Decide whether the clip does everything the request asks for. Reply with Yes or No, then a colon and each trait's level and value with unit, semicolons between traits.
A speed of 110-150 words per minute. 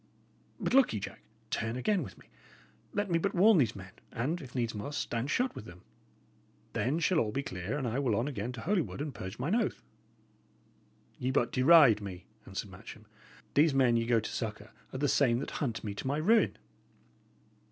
No: fast, 205 wpm